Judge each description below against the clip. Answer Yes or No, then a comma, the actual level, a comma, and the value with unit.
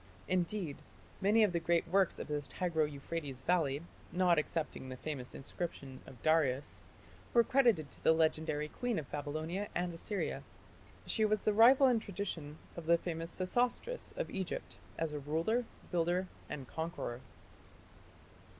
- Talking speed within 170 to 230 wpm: No, average, 150 wpm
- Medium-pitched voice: Yes, medium, 165 Hz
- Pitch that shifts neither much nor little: Yes, average, 4.7 semitones